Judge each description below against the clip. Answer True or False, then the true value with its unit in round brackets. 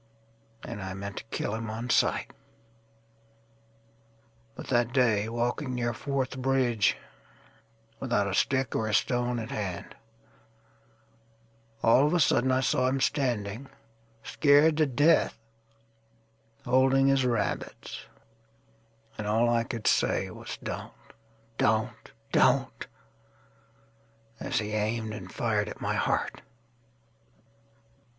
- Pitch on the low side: True (115 Hz)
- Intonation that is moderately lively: False (1.6 semitones)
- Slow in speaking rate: True (100 wpm)